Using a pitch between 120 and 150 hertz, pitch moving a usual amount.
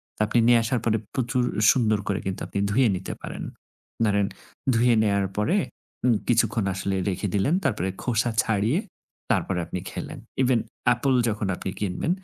No: low, 110 Hz; average, 3.4 semitones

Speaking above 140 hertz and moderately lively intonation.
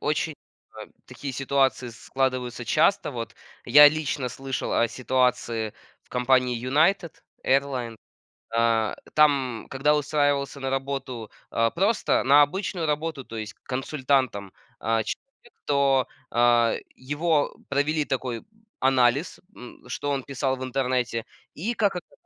No: low, 135 Hz; average, 3.0 semitones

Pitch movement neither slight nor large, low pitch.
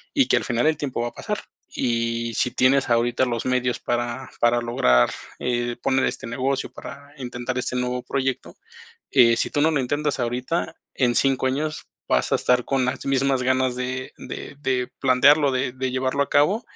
No: narrow, 2.1 semitones; low, 130 Hz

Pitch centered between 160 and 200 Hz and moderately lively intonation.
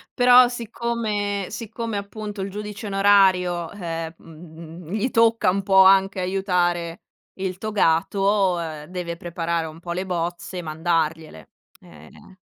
Yes: medium, 185 Hz; average, 3.3 semitones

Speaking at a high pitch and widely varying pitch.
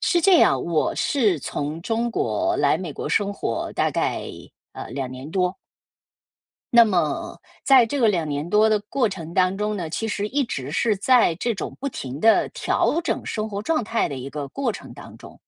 Yes: high, 205 Hz; wide, 6.9 semitones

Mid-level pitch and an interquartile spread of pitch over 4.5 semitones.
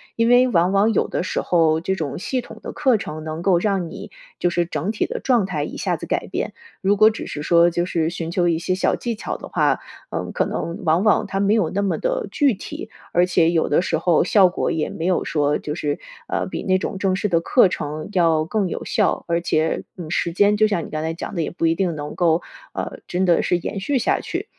No: medium, 175 Hz; average, 3.6 semitones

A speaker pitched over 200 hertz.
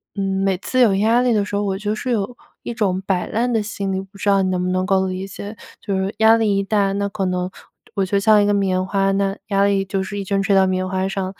No: high, 195 Hz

